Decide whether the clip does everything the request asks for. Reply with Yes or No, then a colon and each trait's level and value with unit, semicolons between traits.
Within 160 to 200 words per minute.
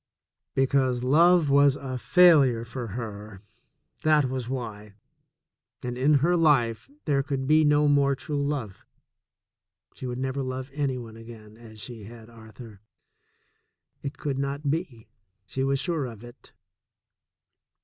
No: average, 140 wpm